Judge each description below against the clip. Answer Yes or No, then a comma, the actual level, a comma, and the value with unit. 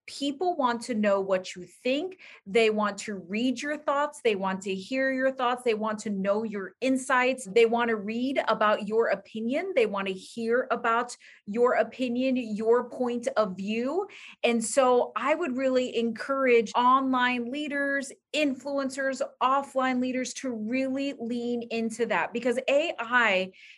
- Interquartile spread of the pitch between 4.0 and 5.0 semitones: No, average, 3.2 semitones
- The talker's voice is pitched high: Yes, high, 245 Hz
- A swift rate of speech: No, average, 155 wpm